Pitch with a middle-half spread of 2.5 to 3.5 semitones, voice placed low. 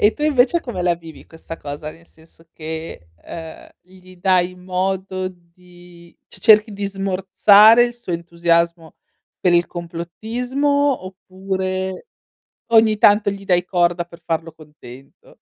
No: average, 2.9 semitones; medium, 185 Hz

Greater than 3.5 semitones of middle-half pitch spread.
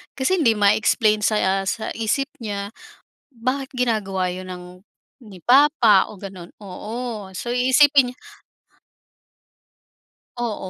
Yes: average, 4.3 semitones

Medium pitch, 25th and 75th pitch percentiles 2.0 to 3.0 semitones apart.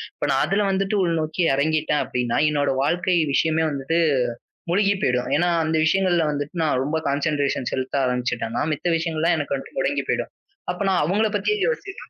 No: medium, 155 Hz; average, 4.1 semitones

